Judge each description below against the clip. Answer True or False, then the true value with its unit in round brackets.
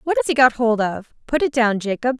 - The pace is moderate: False (275 wpm)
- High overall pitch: True (235 Hz)